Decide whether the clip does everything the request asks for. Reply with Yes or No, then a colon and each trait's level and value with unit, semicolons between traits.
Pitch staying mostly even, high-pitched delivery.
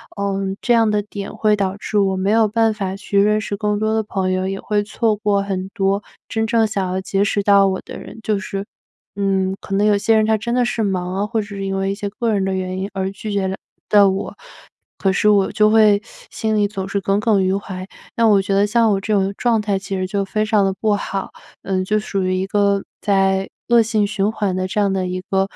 Yes: narrow, 1.7 semitones; high, 200 Hz